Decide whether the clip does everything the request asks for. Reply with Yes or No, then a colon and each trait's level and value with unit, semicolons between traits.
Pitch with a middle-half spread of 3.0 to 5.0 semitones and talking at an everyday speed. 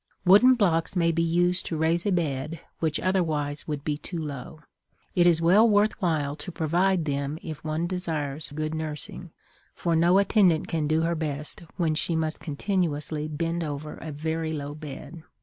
No: narrow, 2.5 semitones; average, 175 wpm